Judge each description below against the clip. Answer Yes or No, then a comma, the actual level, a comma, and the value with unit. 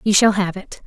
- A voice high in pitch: Yes, high, 195 Hz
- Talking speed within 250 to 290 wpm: Yes, fast, 275 wpm